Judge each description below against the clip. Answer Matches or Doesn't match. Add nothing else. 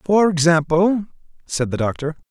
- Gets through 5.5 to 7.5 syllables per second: Doesn't match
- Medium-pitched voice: Matches